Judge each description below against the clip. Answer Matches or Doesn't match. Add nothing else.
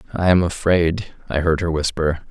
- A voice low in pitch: Matches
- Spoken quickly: Doesn't match